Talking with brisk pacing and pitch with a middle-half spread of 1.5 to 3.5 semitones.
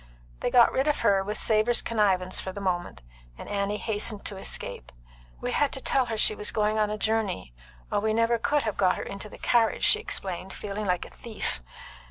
Yes: fast, 210 wpm; average, 2.8 semitones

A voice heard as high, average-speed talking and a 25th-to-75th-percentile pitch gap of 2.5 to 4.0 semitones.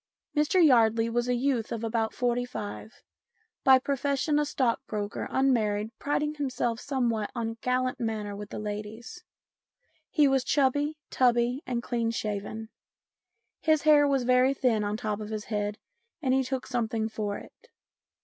Yes: high, 240 Hz; average, 160 wpm; average, 3.5 semitones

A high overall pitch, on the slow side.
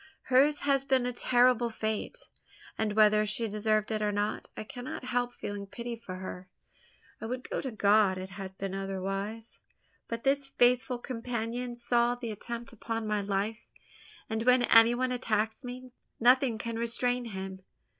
No: high, 230 Hz; average, 160 wpm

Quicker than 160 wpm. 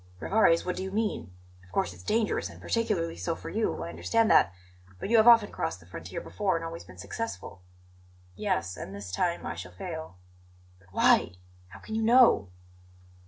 Yes: average, 190 wpm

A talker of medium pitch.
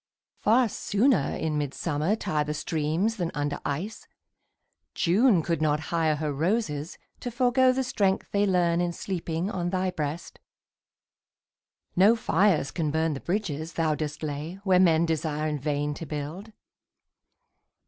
Yes: medium, 165 Hz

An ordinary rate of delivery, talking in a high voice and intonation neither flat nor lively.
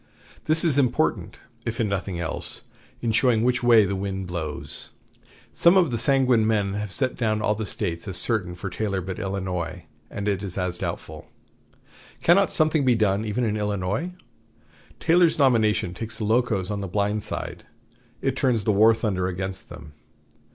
No: average, 170 wpm; low, 105 Hz; average, 4.1 semitones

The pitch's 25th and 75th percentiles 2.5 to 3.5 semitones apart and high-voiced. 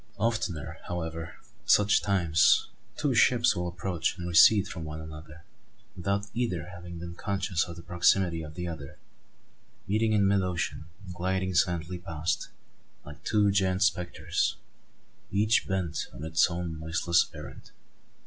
No: average, 3.2 semitones; very low, 90 Hz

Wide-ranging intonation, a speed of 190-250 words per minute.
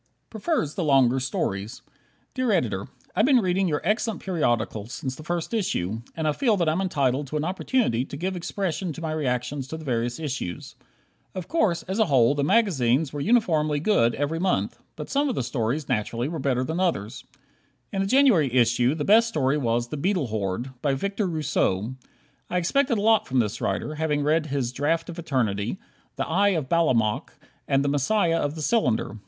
Yes: wide, 6.7 semitones; average, 195 wpm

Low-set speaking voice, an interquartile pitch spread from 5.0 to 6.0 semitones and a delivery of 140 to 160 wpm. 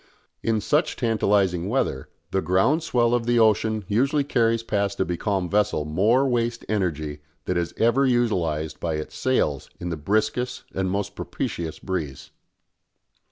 Yes: low, 100 Hz; average, 5.3 semitones; average, 150 wpm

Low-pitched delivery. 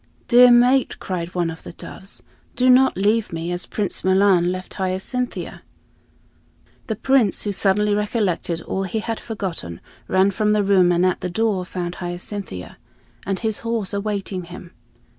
No: high, 195 Hz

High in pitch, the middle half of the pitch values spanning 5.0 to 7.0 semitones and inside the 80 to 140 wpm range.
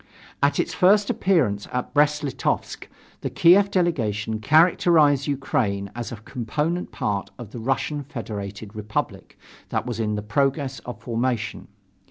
No: low, 130 Hz; wide, 5.6 semitones; slow, 135 wpm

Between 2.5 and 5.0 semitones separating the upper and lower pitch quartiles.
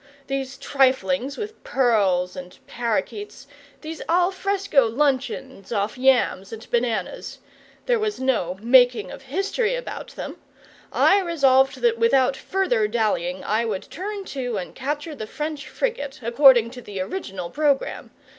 No: wide, 5.4 semitones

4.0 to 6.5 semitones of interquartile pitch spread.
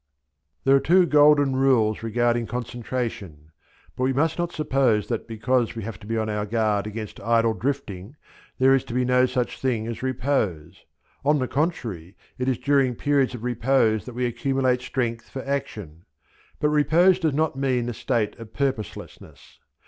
No: average, 3.5 semitones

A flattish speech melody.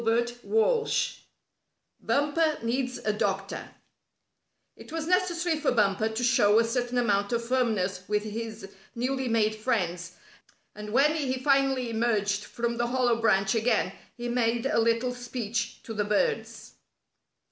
No: average, 3.3 semitones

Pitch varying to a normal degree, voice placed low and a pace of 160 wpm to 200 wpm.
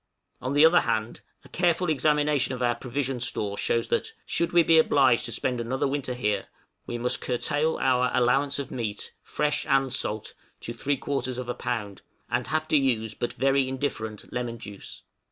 Yes: average, 3.3 semitones; low, 130 Hz; average, 185 wpm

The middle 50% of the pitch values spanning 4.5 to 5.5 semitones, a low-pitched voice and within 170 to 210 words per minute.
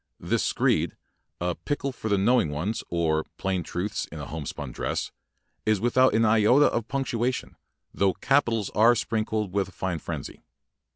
No: average, 4.9 semitones; low, 105 Hz; average, 160 wpm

